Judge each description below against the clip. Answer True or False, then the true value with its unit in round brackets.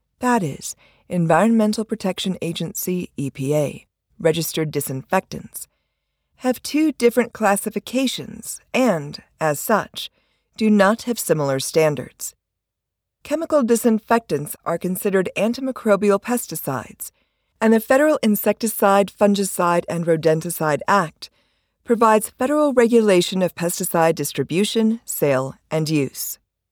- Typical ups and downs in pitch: False (6.1 semitones)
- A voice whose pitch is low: False (190 Hz)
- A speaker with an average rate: False (95 wpm)